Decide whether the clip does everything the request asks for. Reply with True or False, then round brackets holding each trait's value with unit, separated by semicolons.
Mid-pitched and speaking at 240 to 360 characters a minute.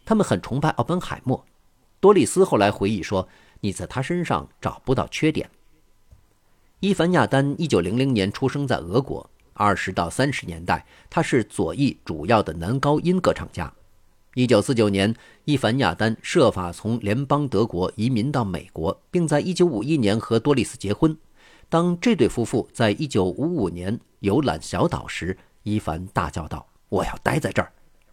False (115 Hz; 260 characters per minute)